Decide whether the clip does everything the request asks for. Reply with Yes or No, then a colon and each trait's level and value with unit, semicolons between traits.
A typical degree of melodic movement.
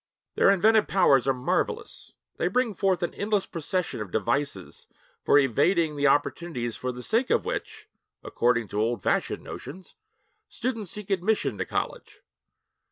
No: wide, 7.8 semitones